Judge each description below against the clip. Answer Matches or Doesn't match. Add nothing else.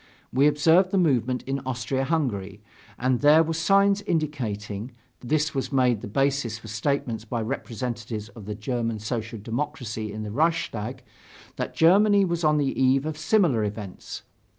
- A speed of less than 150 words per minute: Doesn't match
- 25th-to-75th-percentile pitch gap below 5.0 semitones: Doesn't match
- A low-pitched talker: Matches